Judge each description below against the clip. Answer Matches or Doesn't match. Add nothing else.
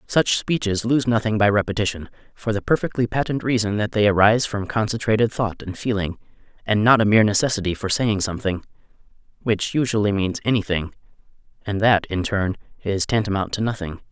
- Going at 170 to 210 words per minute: Doesn't match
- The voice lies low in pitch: Matches